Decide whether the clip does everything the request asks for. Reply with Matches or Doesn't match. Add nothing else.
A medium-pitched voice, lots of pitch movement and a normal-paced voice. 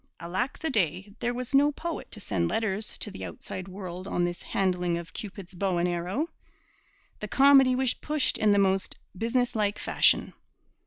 Doesn't match